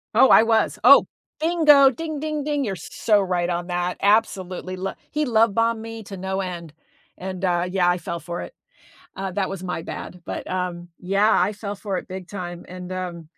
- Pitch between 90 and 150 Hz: No, high, 190 Hz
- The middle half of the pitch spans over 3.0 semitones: Yes, average, 3.8 semitones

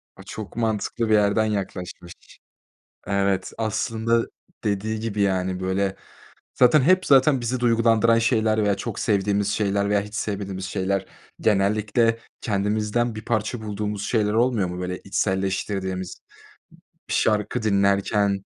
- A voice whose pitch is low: Yes, low, 105 Hz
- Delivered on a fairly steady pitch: Yes, narrow, 2.3 semitones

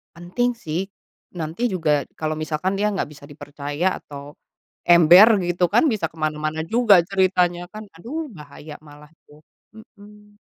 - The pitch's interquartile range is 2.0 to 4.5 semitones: No, average, 5.0 semitones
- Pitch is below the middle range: No, medium, 175 Hz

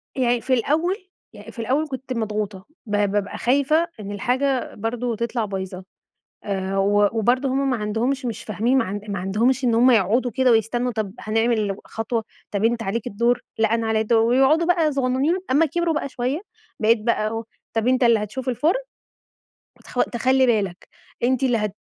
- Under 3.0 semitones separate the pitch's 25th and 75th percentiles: No, average, 3.5 semitones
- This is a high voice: Yes, high, 235 Hz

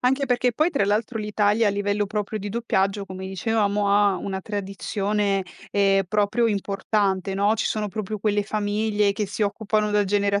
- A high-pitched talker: Yes, high, 205 Hz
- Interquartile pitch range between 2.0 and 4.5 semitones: No, narrow, 1.4 semitones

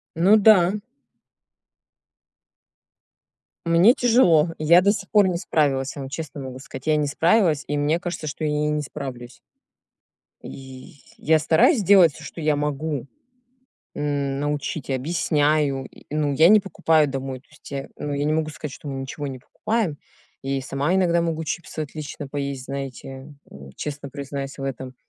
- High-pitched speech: No, medium, 150 Hz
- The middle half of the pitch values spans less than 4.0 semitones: Yes, average, 3.3 semitones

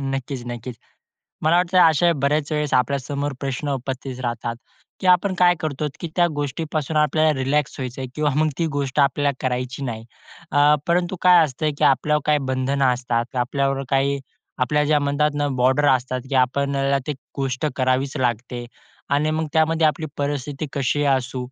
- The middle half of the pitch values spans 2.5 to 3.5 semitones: Yes, average, 2.8 semitones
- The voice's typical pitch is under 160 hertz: Yes, medium, 140 Hz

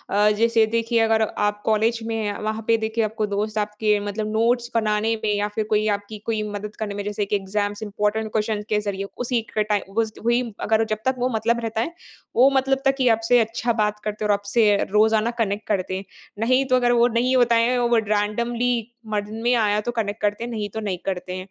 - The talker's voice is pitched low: No, high, 220 Hz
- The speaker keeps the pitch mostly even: Yes, narrow, 1.9 semitones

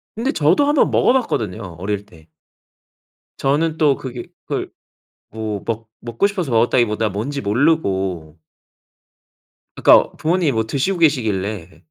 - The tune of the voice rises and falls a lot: Yes, wide, 7.1 semitones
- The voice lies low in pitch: Yes, low, 115 Hz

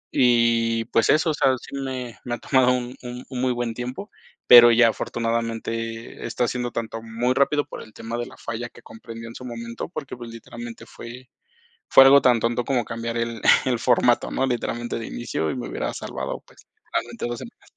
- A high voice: No, low, 120 Hz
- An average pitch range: No, narrow, 1.5 semitones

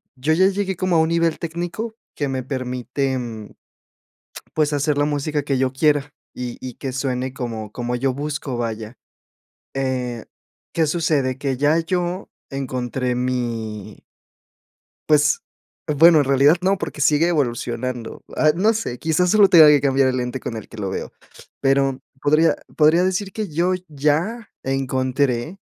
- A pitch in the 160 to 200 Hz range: No, medium, 140 Hz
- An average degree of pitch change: Yes, average, 4.1 semitones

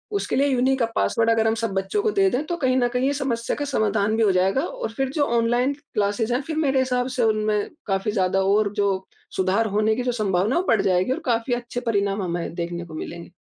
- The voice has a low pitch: No, high, 225 Hz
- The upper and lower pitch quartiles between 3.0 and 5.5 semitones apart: Yes, average, 4.5 semitones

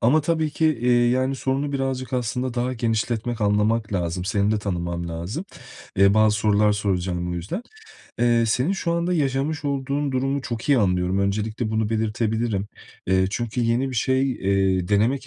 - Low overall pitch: Yes, low, 115 Hz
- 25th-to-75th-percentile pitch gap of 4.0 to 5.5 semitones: Yes, average, 4.7 semitones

